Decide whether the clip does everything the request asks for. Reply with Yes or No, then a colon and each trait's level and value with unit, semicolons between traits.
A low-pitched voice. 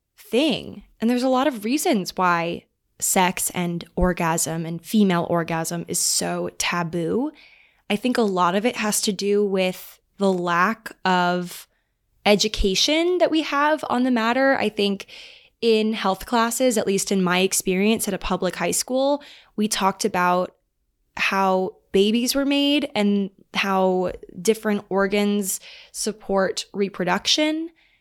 No: high, 205 Hz